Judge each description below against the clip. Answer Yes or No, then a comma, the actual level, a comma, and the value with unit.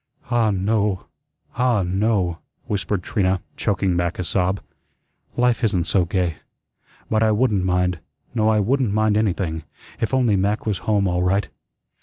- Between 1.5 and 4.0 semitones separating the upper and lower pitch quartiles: Yes, average, 3.1 semitones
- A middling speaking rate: Yes, average, 150 wpm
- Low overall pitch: Yes, low, 100 Hz